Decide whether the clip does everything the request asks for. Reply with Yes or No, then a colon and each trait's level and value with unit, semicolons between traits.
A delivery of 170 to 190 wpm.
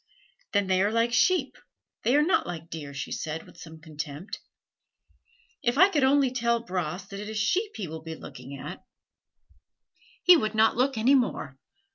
Yes: average, 180 wpm